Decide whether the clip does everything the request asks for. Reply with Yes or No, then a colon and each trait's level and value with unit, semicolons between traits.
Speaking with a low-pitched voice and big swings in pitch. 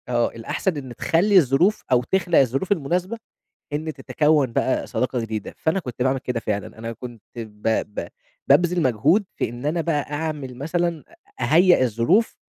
No: medium, 145 Hz; wide, 5.9 semitones